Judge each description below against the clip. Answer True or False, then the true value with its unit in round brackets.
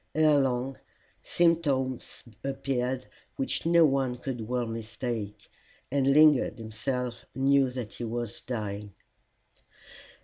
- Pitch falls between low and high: False (130 Hz)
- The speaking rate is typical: False (105 wpm)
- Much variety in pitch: False (2.6 semitones)